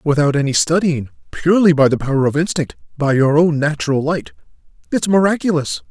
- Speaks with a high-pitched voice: No, medium, 150 Hz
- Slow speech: No, average, 155 wpm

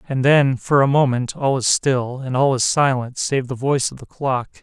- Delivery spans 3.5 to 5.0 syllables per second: Yes, 4.9 syllables/s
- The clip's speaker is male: Yes, male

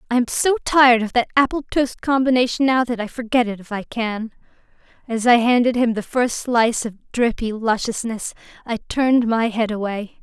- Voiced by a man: No, female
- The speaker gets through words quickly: No, average, 190 wpm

